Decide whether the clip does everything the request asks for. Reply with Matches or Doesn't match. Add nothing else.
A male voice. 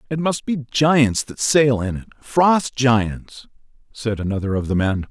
Matches